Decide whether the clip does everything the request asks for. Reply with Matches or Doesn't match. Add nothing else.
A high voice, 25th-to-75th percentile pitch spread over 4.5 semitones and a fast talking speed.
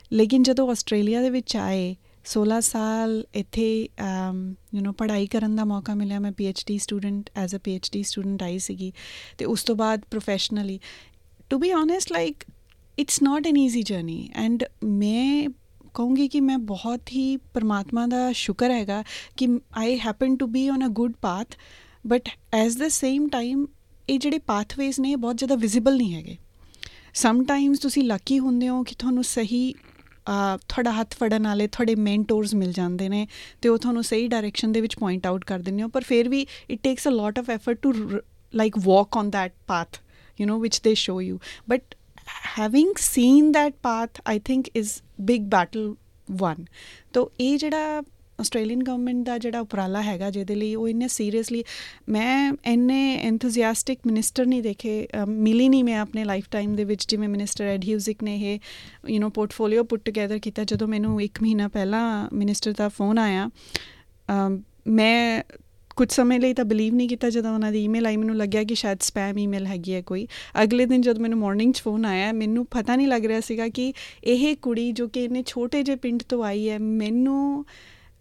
Doesn't match